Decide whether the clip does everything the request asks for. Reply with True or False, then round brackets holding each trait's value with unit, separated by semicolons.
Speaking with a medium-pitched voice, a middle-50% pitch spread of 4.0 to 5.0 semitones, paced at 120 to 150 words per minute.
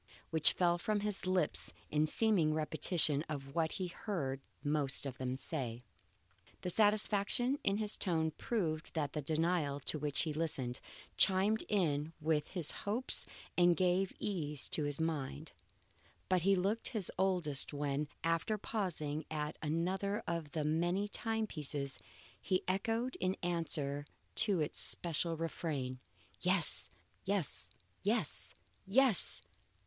True (165 Hz; 4.5 semitones; 135 wpm)